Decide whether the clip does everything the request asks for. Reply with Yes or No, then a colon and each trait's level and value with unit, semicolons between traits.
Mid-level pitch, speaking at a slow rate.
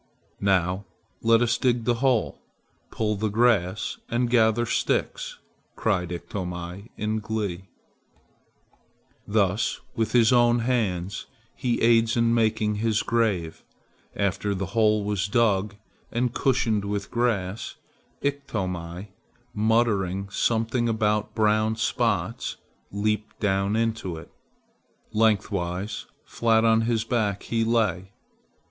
No: low, 110 Hz; slow, 110 wpm